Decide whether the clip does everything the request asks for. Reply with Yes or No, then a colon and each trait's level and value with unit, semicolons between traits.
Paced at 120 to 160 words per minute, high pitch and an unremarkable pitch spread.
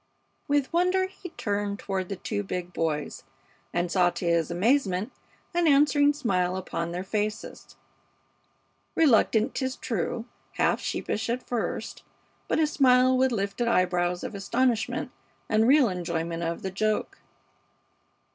No: slow, 135 wpm; high, 210 Hz; wide, 6.3 semitones